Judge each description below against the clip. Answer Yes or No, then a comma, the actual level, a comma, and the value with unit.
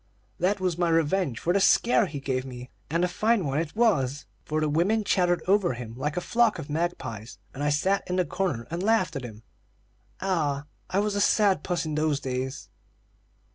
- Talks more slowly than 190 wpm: No, fast, 205 wpm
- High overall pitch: No, medium, 165 Hz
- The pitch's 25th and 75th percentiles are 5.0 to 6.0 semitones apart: Yes, average, 5.3 semitones